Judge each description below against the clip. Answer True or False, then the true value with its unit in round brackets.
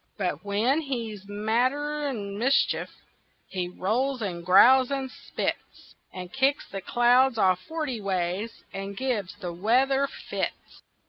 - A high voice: True (225 Hz)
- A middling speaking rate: False (125 wpm)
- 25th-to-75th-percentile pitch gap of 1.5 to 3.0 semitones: False (5.3 semitones)